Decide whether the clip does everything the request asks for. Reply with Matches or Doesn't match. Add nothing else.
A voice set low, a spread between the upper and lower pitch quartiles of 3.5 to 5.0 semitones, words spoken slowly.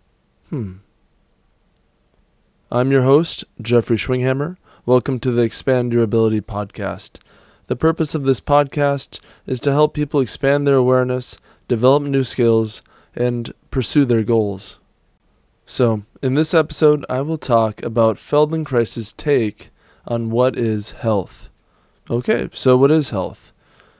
Matches